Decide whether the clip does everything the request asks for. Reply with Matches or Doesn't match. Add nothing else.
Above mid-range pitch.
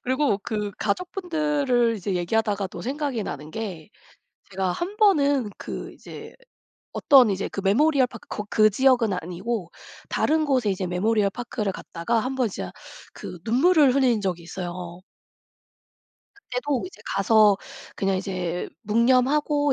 Matches